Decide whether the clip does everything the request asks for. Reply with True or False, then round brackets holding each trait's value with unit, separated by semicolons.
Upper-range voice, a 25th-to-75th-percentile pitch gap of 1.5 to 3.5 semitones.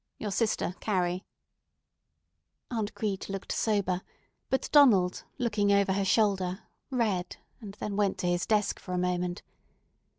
True (200 Hz; 2.8 semitones)